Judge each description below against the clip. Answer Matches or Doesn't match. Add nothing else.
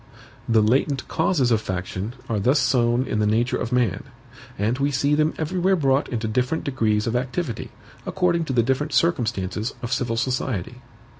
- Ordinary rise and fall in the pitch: Matches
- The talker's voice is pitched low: Matches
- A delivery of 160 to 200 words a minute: Matches